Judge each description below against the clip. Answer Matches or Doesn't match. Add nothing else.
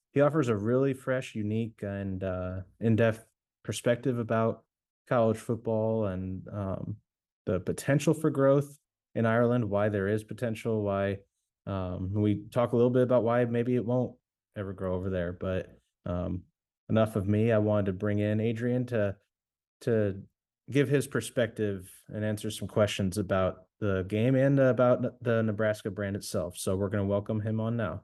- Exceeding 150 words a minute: Matches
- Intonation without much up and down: Doesn't match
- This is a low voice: Matches